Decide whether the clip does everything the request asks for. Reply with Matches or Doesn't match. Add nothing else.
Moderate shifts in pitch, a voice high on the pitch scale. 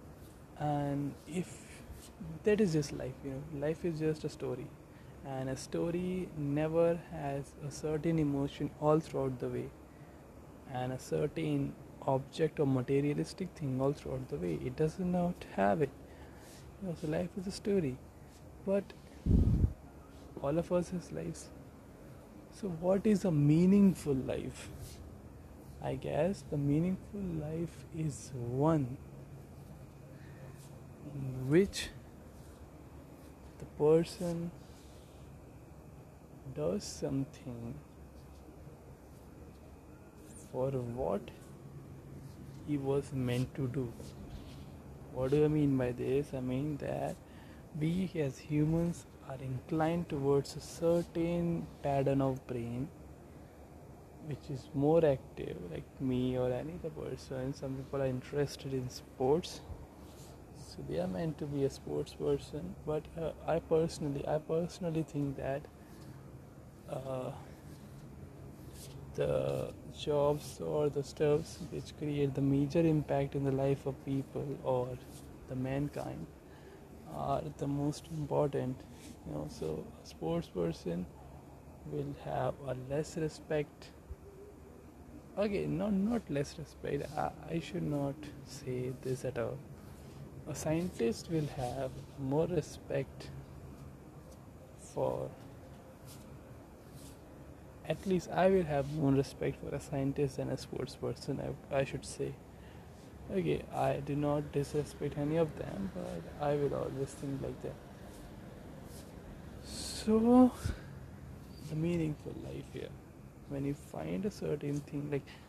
Doesn't match